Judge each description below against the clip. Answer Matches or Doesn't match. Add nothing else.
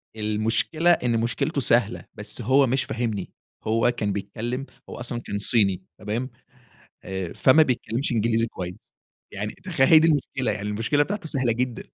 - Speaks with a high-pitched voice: Doesn't match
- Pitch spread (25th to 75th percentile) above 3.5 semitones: Matches